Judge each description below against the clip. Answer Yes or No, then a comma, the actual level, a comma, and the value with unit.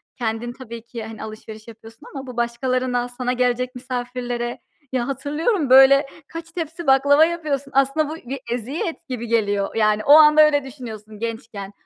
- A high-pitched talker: Yes, very high, 250 Hz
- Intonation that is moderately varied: Yes, average, 3.5 semitones